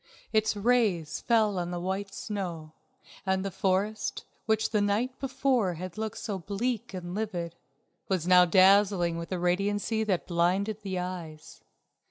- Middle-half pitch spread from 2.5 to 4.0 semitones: Yes, average, 3.3 semitones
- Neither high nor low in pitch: No, high, 195 Hz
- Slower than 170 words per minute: Yes, average, 150 wpm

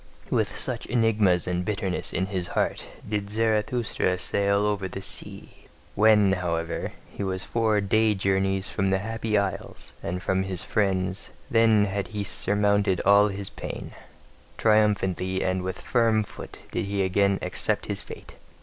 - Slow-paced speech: No, average, 150 wpm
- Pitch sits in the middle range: No, low, 100 Hz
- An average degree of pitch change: No, narrow, 2.1 semitones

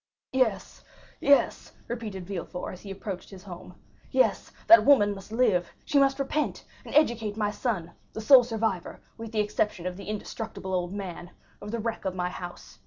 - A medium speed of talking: Yes, average, 175 wpm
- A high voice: Yes, high, 210 Hz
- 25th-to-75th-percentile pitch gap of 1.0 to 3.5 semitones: No, average, 3.9 semitones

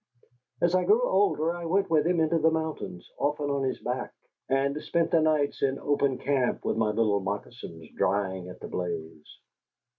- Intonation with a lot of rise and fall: Yes, wide, 7.4 semitones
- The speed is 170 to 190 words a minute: Yes, average, 180 wpm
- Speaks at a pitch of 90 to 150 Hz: Yes, medium, 140 Hz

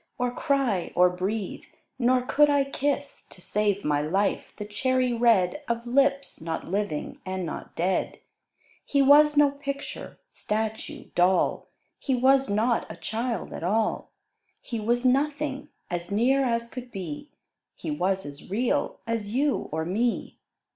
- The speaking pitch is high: Yes, high, 235 Hz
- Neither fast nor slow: Yes, average, 145 wpm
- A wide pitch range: Yes, wide, 6.1 semitones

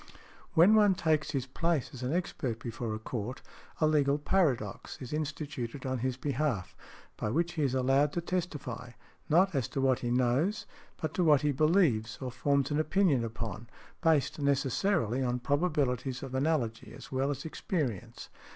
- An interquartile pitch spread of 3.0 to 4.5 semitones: Yes, average, 4.0 semitones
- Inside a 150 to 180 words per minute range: Yes, average, 165 wpm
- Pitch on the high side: No, medium, 140 Hz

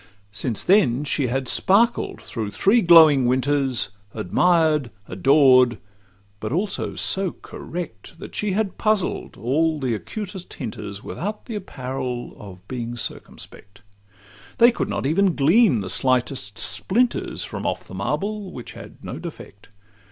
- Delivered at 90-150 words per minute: Yes, slow, 135 wpm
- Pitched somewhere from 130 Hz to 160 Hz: Yes, medium, 140 Hz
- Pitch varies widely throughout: Yes, wide, 7.9 semitones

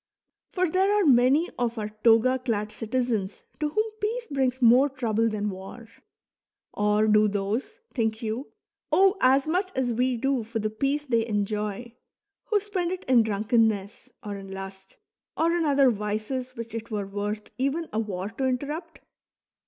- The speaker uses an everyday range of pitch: Yes, average, 4.6 semitones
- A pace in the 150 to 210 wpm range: Yes, average, 165 wpm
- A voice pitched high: Yes, high, 235 Hz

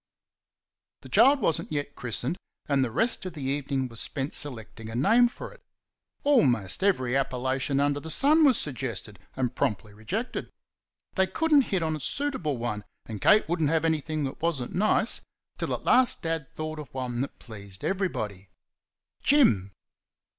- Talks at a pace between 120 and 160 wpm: No, average, 175 wpm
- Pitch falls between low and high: Yes, medium, 145 Hz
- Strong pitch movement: Yes, wide, 7.2 semitones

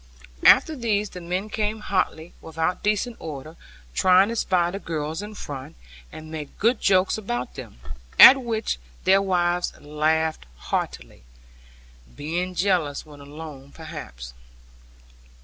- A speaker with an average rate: No, slow, 130 wpm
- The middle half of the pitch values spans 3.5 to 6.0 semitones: Yes, average, 4.8 semitones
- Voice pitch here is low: No, medium, 175 Hz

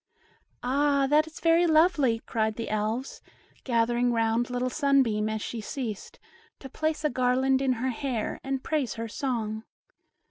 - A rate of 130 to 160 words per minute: Yes, average, 150 wpm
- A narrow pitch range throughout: No, average, 3.6 semitones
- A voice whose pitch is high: Yes, very high, 255 Hz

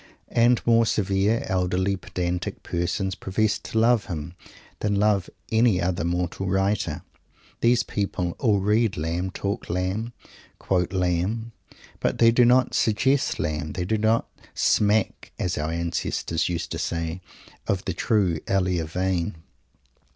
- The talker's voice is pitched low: Yes, very low, 95 Hz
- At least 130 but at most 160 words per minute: Yes, slow, 135 wpm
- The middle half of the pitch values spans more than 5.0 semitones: No, average, 3.7 semitones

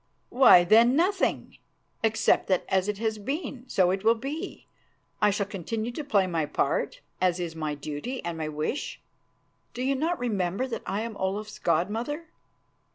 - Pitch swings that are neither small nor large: No, wide, 5.7 semitones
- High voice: Yes, high, 210 Hz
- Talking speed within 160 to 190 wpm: Yes, average, 170 wpm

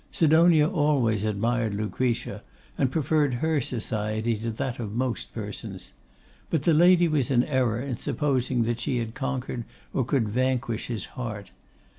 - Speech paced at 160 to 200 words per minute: No, average, 150 wpm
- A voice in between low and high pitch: No, low, 125 Hz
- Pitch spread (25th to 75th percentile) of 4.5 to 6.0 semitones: No, average, 4.1 semitones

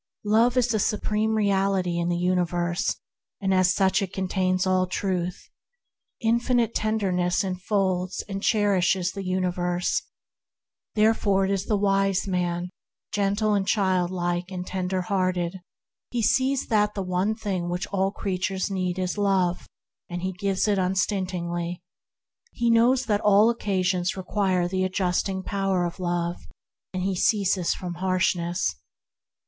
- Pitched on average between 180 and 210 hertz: Yes, high, 190 Hz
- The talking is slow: Yes, slow, 130 wpm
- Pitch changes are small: Yes, narrow, 2.1 semitones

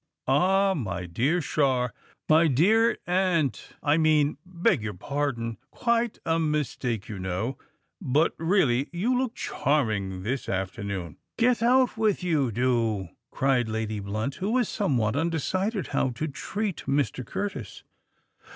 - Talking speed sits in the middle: No, slow, 120 wpm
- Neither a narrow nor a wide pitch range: No, wide, 8.1 semitones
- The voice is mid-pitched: Yes, medium, 145 Hz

